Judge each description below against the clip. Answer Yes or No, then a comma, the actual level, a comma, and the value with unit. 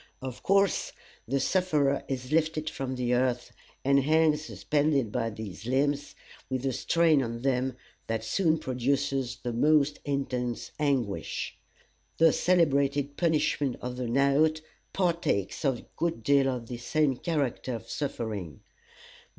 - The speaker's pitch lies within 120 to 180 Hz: Yes, low, 135 Hz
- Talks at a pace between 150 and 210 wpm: No, slow, 135 wpm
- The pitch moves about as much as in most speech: Yes, average, 3.7 semitones